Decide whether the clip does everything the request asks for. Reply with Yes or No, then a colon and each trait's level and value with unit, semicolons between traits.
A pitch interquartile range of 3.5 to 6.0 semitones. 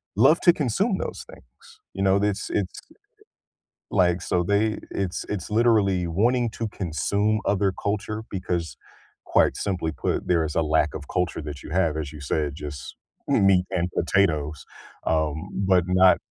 Yes: average, 4.2 semitones